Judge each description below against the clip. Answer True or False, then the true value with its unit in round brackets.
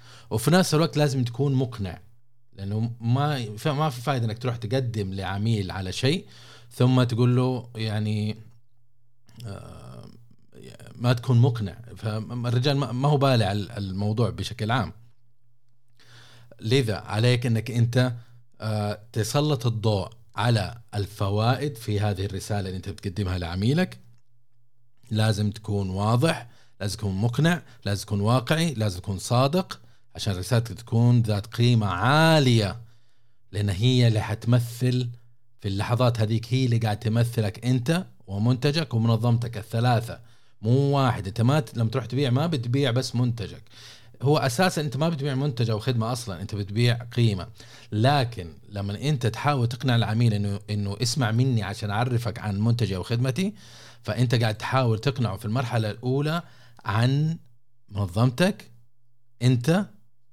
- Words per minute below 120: False (125 wpm)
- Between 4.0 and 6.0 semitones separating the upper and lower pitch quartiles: False (2.8 semitones)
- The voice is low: True (120 Hz)